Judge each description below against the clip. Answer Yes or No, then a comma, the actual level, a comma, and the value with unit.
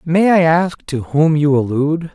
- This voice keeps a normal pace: Yes, average, 195 wpm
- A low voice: No, medium, 155 Hz